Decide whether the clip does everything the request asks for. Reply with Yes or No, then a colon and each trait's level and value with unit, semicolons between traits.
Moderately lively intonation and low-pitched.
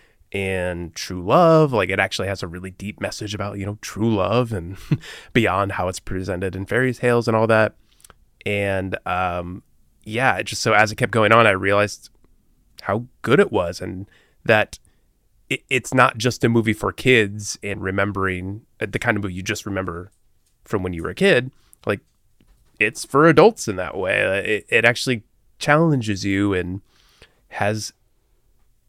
Yes: average, 3.5 semitones; low, 105 Hz